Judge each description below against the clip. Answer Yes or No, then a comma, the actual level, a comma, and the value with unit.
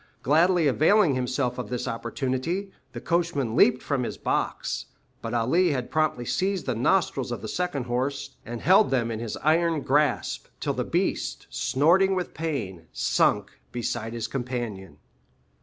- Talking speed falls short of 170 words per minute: Yes, average, 155 wpm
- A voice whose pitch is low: Yes, low, 130 Hz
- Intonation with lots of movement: Yes, wide, 5.7 semitones